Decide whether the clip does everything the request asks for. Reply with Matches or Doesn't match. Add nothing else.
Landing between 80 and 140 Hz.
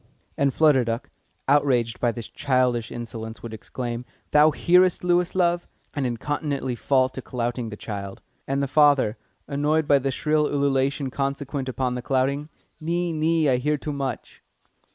Matches